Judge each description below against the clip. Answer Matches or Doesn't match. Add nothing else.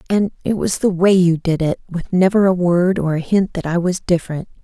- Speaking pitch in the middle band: Matches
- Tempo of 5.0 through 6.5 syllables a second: Matches